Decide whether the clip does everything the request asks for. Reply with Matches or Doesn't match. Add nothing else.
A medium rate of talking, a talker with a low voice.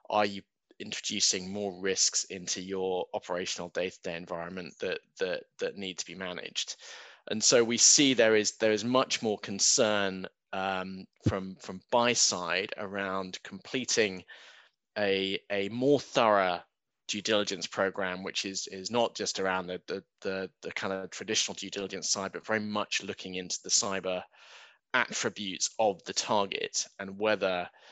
Matches